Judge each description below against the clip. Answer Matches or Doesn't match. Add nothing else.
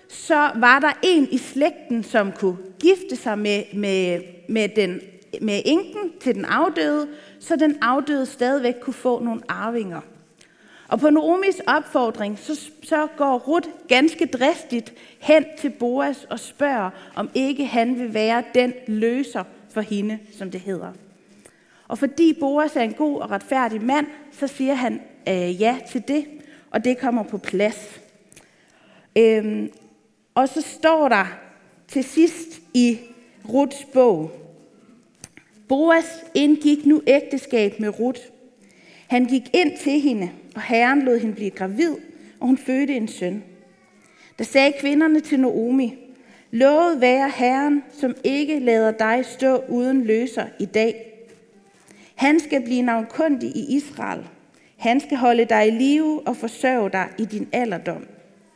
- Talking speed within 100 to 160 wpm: Matches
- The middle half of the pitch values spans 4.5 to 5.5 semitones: Matches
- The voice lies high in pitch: Matches